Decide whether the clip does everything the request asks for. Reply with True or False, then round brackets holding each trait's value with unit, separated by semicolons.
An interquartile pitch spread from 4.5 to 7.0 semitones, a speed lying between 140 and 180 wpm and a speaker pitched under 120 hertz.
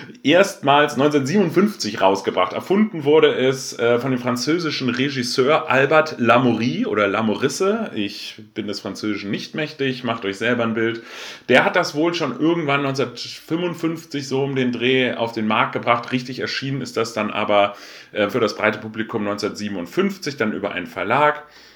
False (5.4 semitones; 150 wpm; 125 Hz)